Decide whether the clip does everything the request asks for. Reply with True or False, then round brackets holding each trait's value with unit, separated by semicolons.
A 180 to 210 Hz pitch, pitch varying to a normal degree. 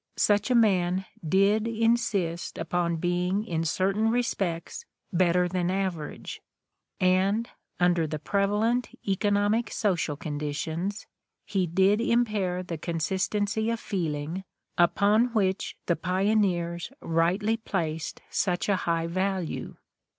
True (185 Hz; 3.4 semitones)